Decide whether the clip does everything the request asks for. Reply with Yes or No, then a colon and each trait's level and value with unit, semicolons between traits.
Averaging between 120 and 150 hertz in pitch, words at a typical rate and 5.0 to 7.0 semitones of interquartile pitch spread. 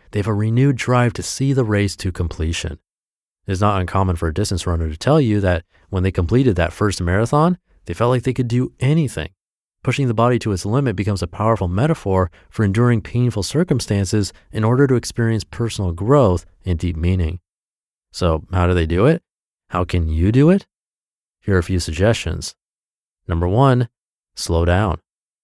No: low, 100 Hz; average, 185 wpm; wide, 5.5 semitones